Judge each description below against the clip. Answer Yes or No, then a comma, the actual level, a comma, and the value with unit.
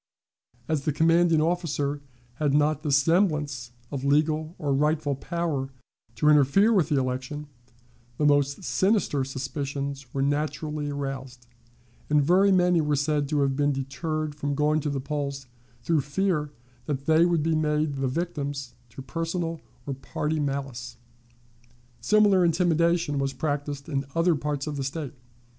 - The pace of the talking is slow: No, average, 150 wpm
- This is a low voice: No, medium, 150 Hz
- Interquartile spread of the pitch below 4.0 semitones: Yes, narrow, 2.5 semitones